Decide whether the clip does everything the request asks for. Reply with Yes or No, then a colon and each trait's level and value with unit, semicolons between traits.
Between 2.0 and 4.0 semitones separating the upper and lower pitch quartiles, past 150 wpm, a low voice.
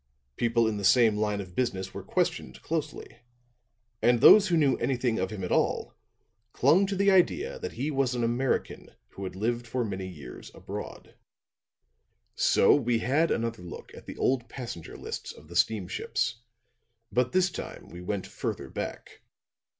No: average, 5.3 semitones; average, 165 wpm; low, 120 Hz